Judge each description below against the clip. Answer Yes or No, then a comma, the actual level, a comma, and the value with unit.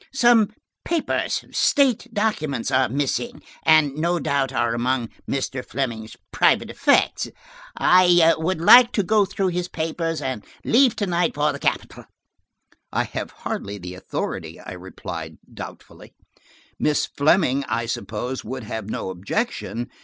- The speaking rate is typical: No, slow, 130 wpm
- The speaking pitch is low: No, medium, 150 Hz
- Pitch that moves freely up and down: Yes, wide, 6.8 semitones